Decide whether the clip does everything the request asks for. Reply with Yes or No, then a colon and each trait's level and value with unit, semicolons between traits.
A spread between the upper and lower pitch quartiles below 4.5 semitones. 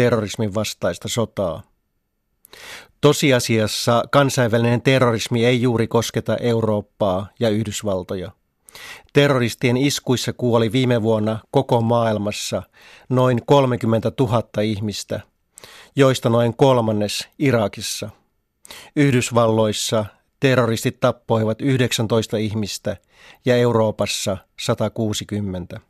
Yes: narrow, 2.6 semitones